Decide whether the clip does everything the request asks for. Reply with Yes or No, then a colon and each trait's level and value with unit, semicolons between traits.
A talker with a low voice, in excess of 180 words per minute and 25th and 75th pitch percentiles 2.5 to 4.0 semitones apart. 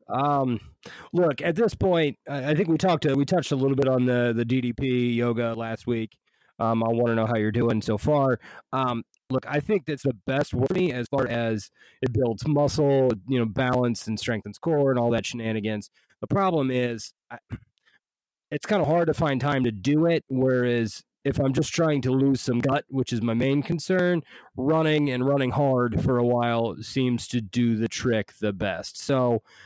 Yes: low, 130 Hz; fast, 205 wpm; average, 3.5 semitones